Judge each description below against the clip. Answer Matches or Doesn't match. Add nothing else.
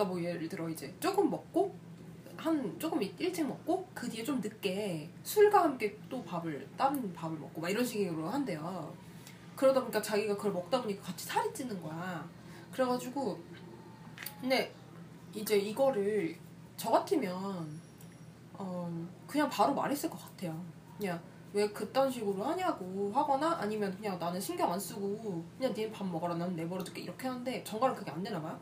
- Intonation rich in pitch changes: Matches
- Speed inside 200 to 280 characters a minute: Doesn't match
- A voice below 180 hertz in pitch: Doesn't match